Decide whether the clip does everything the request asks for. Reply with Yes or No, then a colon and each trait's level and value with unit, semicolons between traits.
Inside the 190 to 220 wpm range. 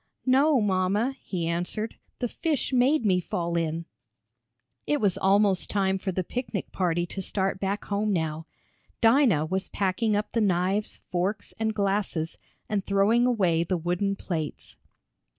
No: average, 150 wpm